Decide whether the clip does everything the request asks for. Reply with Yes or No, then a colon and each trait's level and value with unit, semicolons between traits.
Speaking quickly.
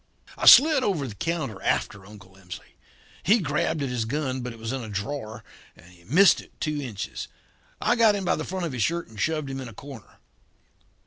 Yes: fast, 215 wpm